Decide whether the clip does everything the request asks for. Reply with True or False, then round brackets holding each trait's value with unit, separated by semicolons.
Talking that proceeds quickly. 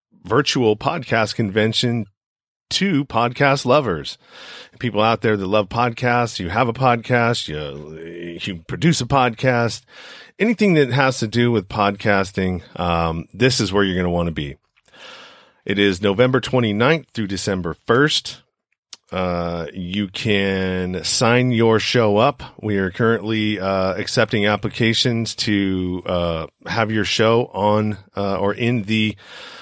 False (140 wpm)